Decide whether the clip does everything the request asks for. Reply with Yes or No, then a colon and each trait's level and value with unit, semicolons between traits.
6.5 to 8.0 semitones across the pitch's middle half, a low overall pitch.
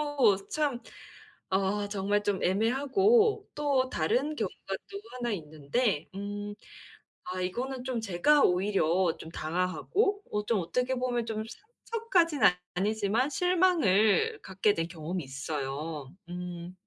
No: wide, 6.9 semitones; high, 205 Hz